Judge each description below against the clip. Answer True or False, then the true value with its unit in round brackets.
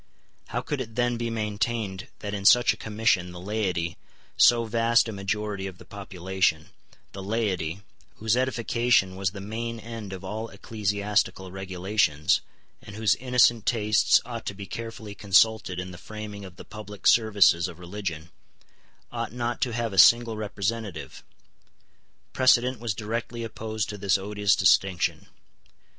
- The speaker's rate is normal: True (150 wpm)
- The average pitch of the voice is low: True (105 Hz)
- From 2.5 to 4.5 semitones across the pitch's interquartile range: True (3.1 semitones)